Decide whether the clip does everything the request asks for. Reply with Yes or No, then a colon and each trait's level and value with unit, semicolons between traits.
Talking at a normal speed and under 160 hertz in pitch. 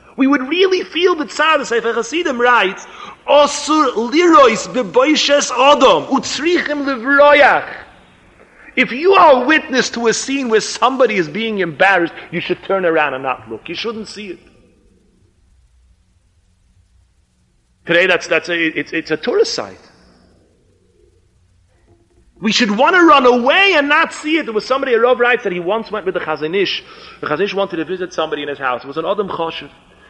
No: average, 165 wpm; high, 220 Hz